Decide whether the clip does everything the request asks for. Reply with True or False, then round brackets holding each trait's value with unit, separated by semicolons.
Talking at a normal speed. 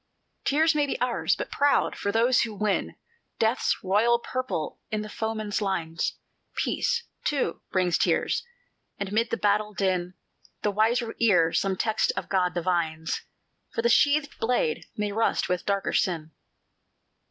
True (150 wpm)